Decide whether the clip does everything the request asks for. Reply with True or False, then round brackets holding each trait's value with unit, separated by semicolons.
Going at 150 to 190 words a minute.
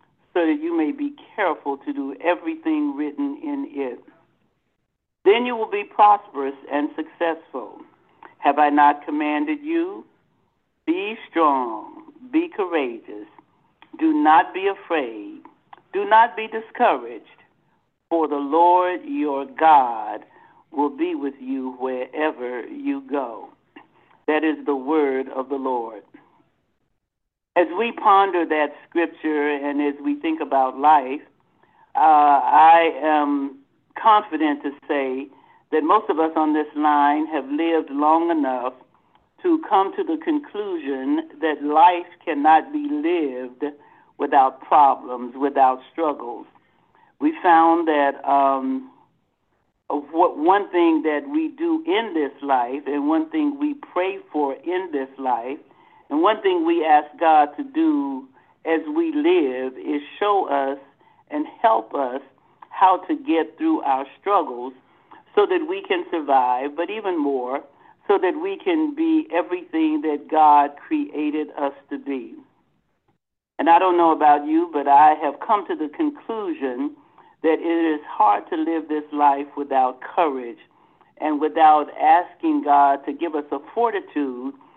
False (135 wpm)